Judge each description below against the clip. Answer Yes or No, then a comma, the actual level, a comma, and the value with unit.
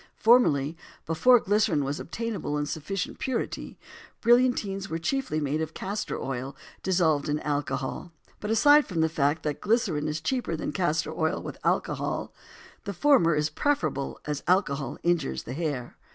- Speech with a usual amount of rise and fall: No, wide, 5.9 semitones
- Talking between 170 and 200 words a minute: No, average, 150 wpm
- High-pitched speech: No, medium, 160 Hz